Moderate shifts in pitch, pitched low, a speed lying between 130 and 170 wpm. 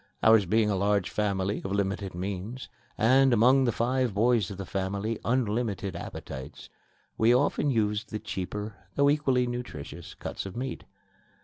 Yes: average, 3.9 semitones; low, 110 Hz; average, 150 wpm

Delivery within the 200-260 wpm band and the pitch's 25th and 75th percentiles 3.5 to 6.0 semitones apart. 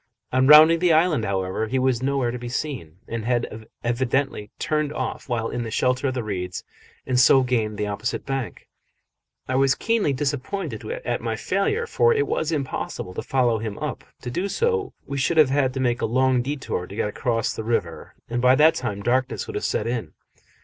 Yes: fast, 205 wpm; average, 4.1 semitones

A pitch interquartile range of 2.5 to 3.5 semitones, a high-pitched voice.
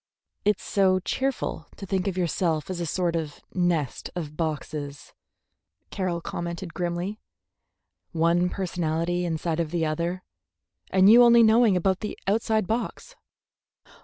No: average, 2.9 semitones; medium, 175 Hz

